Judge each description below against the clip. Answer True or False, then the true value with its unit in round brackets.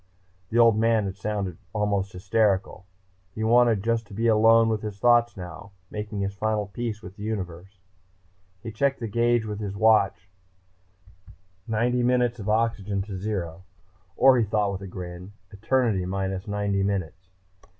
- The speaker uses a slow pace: False (160 wpm)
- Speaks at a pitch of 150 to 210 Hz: False (105 Hz)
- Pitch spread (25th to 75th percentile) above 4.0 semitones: False (2.7 semitones)